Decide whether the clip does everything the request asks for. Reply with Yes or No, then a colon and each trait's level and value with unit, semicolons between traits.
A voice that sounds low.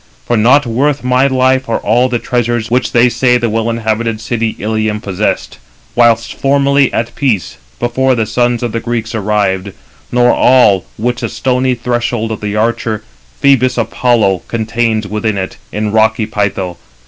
Yes: low, 115 Hz